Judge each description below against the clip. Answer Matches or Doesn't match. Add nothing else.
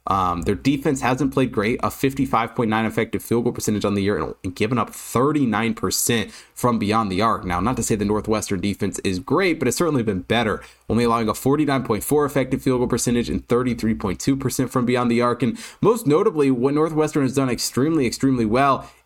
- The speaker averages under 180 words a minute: Doesn't match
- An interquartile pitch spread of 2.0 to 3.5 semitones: Doesn't match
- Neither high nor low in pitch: Doesn't match